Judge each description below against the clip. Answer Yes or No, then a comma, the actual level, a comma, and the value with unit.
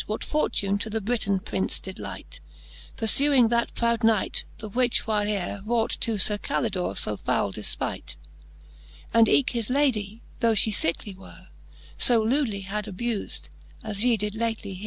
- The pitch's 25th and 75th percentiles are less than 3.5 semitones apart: Yes, average, 2.7 semitones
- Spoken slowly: No, average, 155 wpm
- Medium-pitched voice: No, high, 215 Hz